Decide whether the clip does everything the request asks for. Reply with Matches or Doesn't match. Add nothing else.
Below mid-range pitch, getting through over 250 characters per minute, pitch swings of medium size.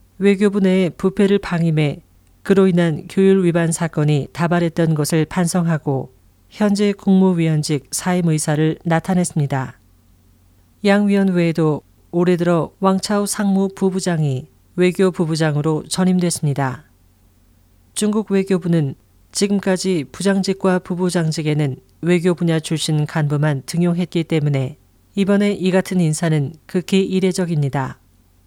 Doesn't match